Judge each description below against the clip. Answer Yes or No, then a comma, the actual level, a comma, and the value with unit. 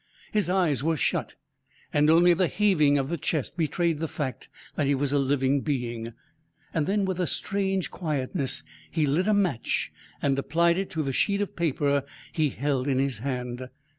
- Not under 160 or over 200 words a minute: Yes, average, 180 wpm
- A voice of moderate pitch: Yes, medium, 150 Hz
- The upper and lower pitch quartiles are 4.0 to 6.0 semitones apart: Yes, average, 4.4 semitones